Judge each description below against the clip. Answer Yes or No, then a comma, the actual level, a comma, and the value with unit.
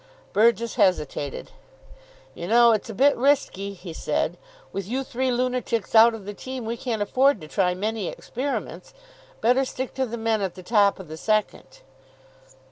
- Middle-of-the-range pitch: No, high, 225 Hz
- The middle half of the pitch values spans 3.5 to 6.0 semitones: Yes, average, 4.3 semitones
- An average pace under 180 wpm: Yes, average, 170 wpm